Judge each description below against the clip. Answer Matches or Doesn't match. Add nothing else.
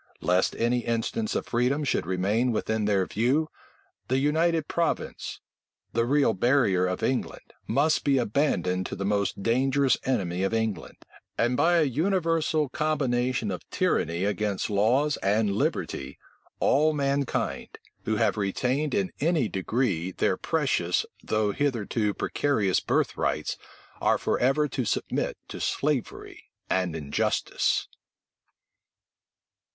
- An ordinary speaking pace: Doesn't match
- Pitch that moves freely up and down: Matches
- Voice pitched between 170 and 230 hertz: Doesn't match